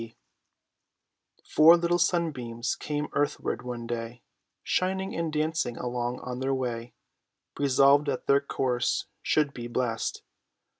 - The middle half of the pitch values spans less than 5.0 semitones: Yes, average, 4.0 semitones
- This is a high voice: No, low, 130 Hz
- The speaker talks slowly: Yes, slow, 130 wpm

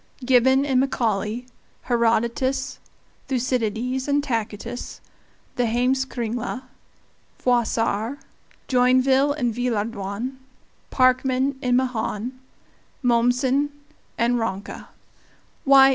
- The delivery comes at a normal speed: No, slow, 75 wpm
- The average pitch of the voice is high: Yes, high, 245 Hz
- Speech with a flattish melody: Yes, narrow, 2.2 semitones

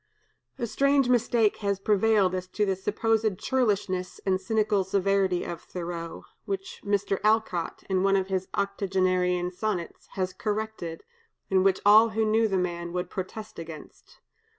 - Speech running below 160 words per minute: Yes, average, 150 wpm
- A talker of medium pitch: No, high, 195 Hz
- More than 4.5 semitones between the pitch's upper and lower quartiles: No, average, 2.8 semitones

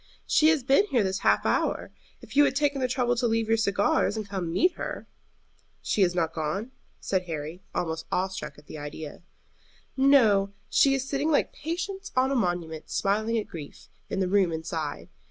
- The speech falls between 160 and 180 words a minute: No, average, 195 wpm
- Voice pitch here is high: Yes, high, 205 Hz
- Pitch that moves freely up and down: Yes, wide, 7.4 semitones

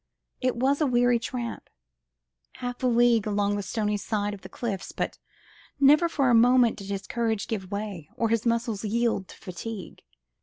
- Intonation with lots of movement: No, average, 3.1 semitones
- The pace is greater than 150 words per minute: Yes, average, 180 wpm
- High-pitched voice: Yes, high, 230 Hz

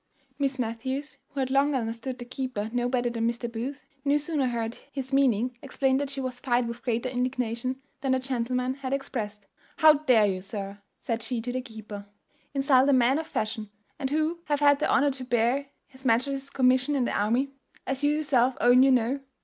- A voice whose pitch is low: No, very high, 255 Hz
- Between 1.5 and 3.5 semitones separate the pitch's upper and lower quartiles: Yes, narrow, 2.6 semitones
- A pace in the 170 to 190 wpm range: No, average, 200 wpm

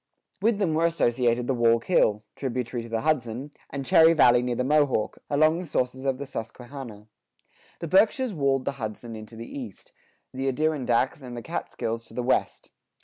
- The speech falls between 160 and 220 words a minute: Yes, average, 180 wpm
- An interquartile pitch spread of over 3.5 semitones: Yes, average, 4.2 semitones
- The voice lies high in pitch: No, low, 130 Hz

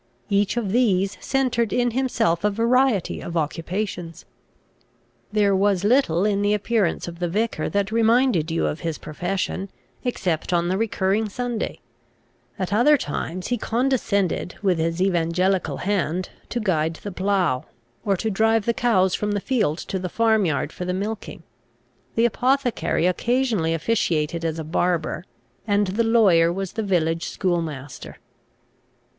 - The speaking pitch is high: Yes, high, 195 Hz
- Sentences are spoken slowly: No, average, 150 wpm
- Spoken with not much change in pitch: No, average, 4.7 semitones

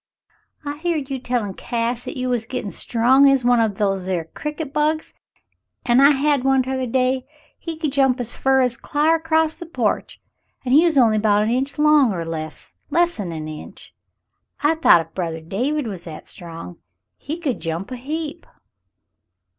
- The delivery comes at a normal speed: Yes, average, 185 wpm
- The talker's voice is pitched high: Yes, very high, 255 Hz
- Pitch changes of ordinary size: No, wide, 6.1 semitones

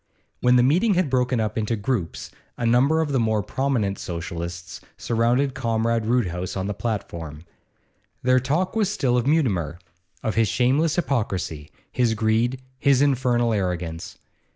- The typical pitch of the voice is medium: No, low, 115 Hz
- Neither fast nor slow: Yes, average, 150 wpm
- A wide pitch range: No, average, 4.8 semitones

